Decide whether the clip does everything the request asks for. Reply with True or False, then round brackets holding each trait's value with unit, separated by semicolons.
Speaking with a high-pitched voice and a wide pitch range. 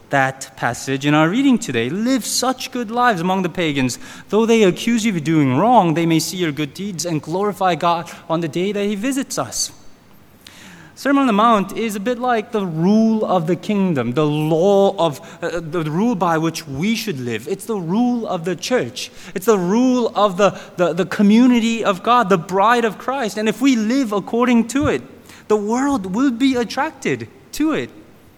True (200 Hz; 5.8 semitones)